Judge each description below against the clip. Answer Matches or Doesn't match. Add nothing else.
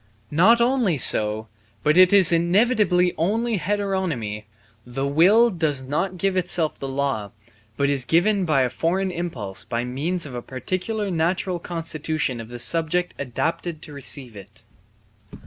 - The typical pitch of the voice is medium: Matches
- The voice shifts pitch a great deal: Matches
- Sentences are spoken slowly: Doesn't match